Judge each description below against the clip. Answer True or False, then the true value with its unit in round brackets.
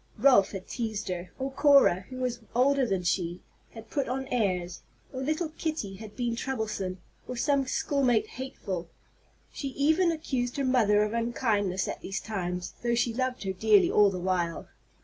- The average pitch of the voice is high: True (230 Hz)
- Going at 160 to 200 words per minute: True (170 wpm)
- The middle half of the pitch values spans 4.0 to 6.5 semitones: True (5.5 semitones)